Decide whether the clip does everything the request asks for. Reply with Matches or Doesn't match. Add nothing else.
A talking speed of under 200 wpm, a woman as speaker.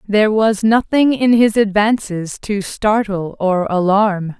Matches